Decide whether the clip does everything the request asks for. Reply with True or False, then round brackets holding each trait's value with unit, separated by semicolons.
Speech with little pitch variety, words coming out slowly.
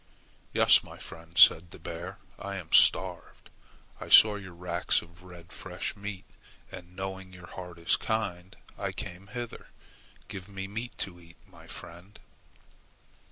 False (2.2 semitones; 150 wpm)